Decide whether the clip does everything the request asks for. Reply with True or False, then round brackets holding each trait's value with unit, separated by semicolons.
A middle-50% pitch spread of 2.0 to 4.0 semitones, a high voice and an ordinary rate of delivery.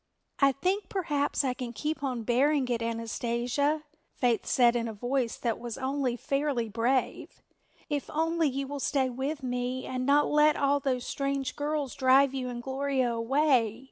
True (2.8 semitones; 265 Hz; 170 wpm)